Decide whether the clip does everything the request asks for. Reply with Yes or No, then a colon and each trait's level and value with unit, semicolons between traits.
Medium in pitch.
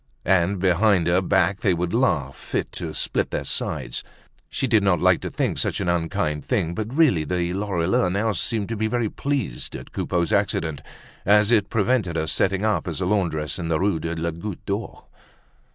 No: very low, 95 Hz